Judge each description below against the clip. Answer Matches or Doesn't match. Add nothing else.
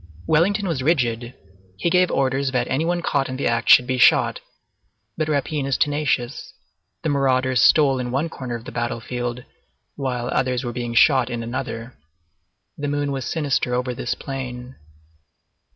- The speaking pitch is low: Matches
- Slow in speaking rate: Doesn't match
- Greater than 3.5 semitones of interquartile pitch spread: Doesn't match